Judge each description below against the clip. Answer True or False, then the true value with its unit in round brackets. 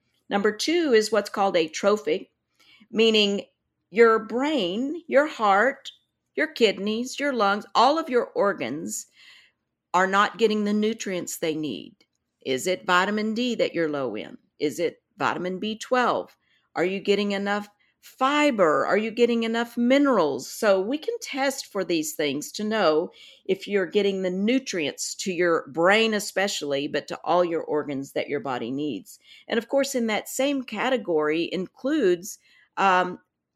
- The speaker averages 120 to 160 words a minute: True (150 wpm)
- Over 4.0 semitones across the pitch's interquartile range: True (5.2 semitones)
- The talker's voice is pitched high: True (205 Hz)